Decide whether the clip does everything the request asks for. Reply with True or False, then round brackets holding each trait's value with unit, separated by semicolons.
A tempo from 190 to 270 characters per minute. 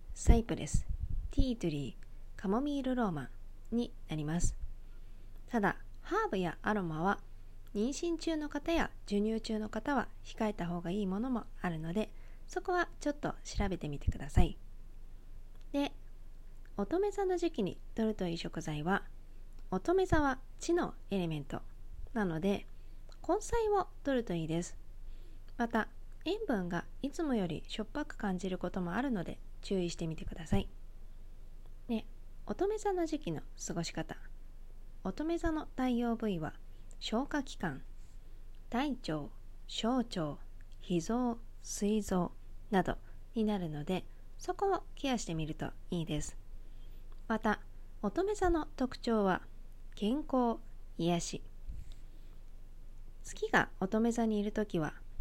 True (250 characters per minute)